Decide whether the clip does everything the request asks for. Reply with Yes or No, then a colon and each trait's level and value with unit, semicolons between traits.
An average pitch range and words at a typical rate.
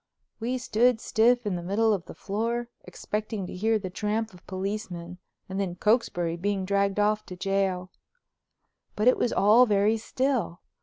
Yes: average, 3.0 semitones; average, 165 wpm